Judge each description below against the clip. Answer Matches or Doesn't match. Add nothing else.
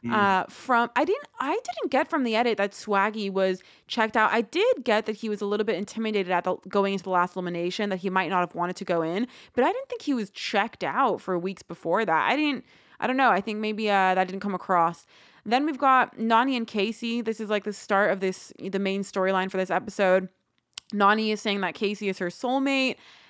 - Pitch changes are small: Doesn't match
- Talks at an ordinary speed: Doesn't match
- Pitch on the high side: Matches